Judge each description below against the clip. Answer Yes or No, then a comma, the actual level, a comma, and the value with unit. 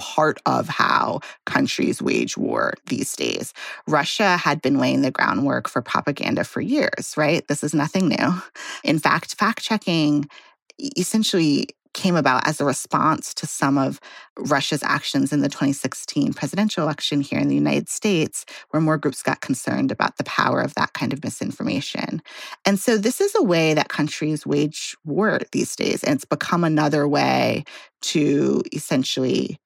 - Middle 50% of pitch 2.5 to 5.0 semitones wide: Yes, average, 4.3 semitones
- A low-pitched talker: No, medium, 150 Hz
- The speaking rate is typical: Yes, average, 160 wpm